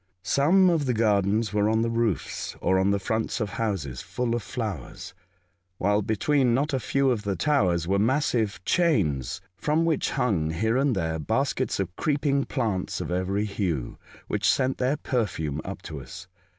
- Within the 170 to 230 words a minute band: Yes, average, 175 wpm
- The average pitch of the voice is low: Yes, low, 110 Hz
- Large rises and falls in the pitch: Yes, wide, 5.8 semitones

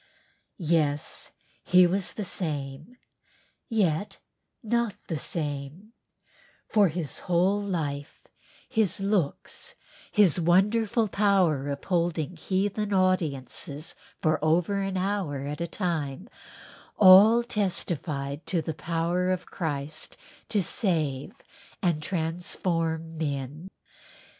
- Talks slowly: Yes, slow, 100 wpm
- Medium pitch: Yes, medium, 175 Hz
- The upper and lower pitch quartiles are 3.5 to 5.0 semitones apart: Yes, average, 4.2 semitones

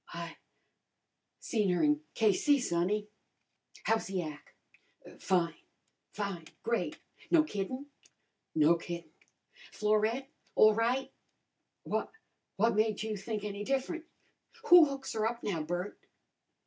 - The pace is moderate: No, slow, 115 wpm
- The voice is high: Yes, high, 210 Hz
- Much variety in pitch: No, average, 5.0 semitones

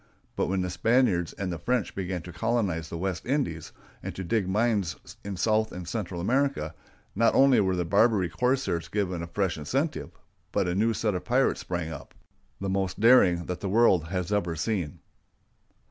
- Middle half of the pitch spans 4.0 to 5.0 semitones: Yes, average, 4.7 semitones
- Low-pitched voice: Yes, very low, 95 Hz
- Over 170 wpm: Yes, average, 185 wpm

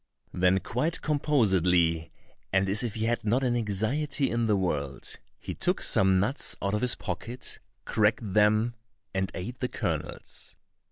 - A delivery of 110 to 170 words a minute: Yes, average, 155 wpm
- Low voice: Yes, low, 105 Hz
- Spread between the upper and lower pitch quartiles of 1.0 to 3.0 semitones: No, average, 4.2 semitones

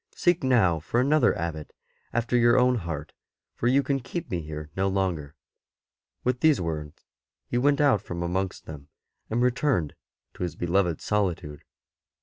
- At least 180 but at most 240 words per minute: No, average, 155 wpm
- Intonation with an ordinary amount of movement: No, wide, 7.3 semitones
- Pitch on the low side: Yes, very low, 95 Hz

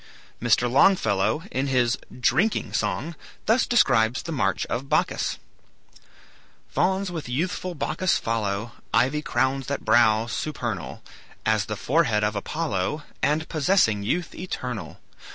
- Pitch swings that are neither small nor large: No, wide, 6.5 semitones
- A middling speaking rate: No, slow, 120 wpm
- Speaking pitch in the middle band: No, low, 130 Hz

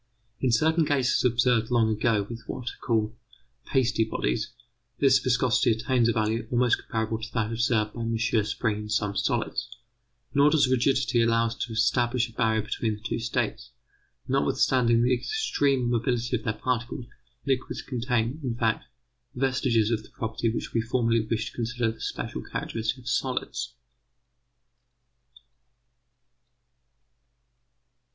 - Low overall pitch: Yes, low, 115 Hz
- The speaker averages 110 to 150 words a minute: Yes, average, 145 wpm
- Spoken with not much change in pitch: Yes, narrow, 2.1 semitones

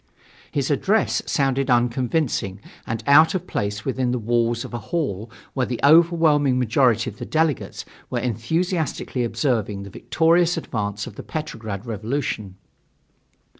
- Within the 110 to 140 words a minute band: Yes, slow, 135 wpm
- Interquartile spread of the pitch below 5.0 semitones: No, wide, 5.5 semitones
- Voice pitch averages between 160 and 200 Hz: No, low, 125 Hz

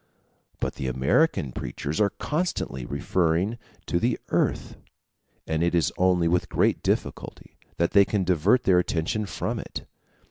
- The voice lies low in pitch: Yes, very low, 90 Hz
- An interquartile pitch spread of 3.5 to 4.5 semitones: Yes, average, 4.2 semitones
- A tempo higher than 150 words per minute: No, average, 145 wpm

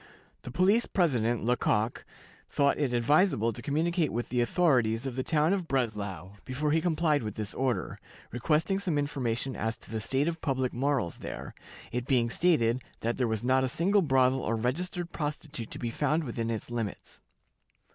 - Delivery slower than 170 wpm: No, average, 175 wpm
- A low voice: Yes, low, 130 Hz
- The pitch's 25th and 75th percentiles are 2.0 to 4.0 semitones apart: No, average, 4.9 semitones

